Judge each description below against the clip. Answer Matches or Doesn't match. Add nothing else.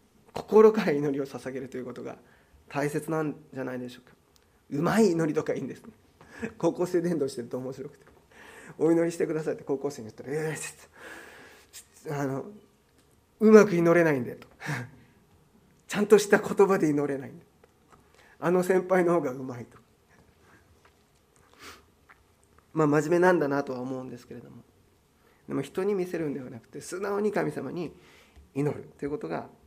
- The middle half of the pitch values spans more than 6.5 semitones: Doesn't match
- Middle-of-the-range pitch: Matches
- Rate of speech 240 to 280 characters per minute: Doesn't match